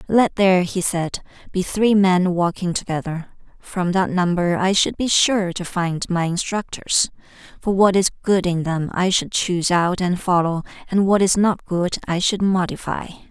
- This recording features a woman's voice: Yes, female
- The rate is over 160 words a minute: Yes, average, 180 wpm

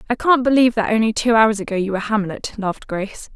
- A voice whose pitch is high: Yes, high, 220 Hz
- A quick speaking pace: Yes, fast, 230 wpm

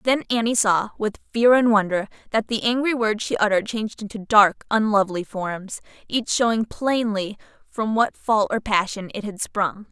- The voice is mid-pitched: No, high, 215 Hz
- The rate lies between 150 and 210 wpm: Yes, average, 175 wpm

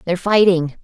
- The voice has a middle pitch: Yes, medium, 180 Hz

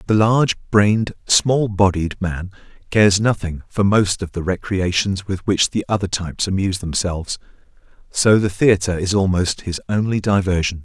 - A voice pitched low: Yes, very low, 95 Hz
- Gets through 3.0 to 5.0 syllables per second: Yes, 4.9 syllables/s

